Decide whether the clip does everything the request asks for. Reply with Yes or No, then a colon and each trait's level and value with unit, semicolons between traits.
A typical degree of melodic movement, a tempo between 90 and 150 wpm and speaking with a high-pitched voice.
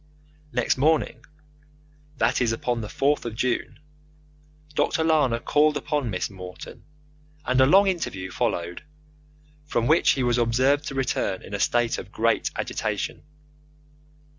No: average, 4.4 semitones; average, 140 wpm; low, 125 Hz